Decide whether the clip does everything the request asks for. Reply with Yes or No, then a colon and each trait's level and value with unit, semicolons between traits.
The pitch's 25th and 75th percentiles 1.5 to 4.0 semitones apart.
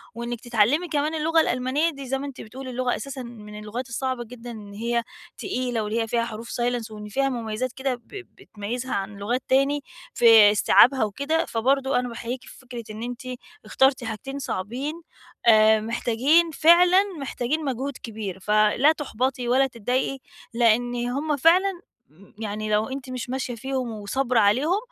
Yes: average, 3.4 semitones